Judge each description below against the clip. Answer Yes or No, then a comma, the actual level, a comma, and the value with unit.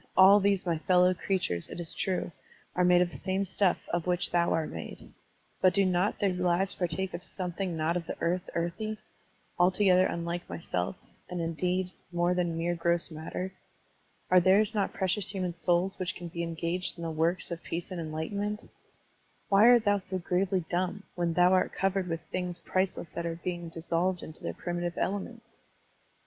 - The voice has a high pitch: No, medium, 180 Hz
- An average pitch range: No, narrow, 1.9 semitones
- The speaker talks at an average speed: Yes, average, 185 wpm